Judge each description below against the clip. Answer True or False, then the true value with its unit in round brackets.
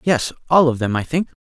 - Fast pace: True (250 wpm)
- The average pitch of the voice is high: False (140 Hz)